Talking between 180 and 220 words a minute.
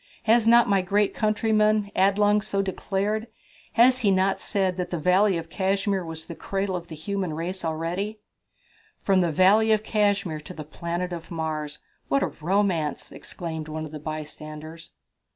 No: average, 165 wpm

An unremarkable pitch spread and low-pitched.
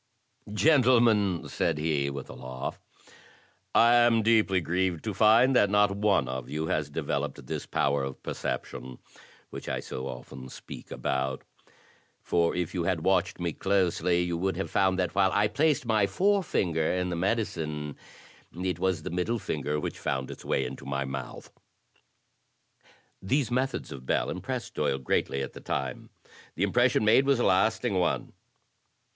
No: wide, 6.4 semitones; very low, 90 Hz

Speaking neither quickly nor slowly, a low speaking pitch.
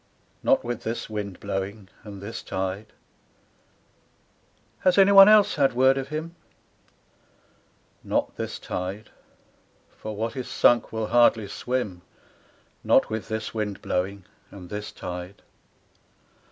No: slow, 125 wpm; low, 110 Hz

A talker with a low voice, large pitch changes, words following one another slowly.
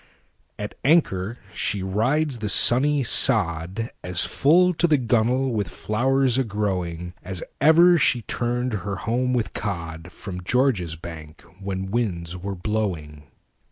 Yes: low, 105 Hz; wide, 6.0 semitones; slow, 120 wpm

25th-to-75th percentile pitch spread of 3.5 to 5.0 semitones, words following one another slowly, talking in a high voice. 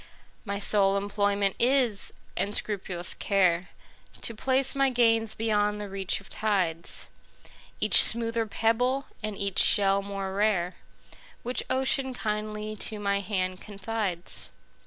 No: narrow, 2.5 semitones; slow, 115 wpm; high, 210 Hz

